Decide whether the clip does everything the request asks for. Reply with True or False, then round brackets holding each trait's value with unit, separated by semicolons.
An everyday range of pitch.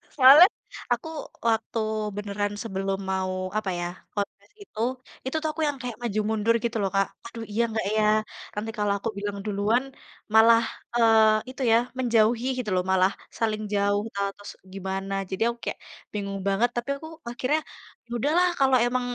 True (3.1 semitones)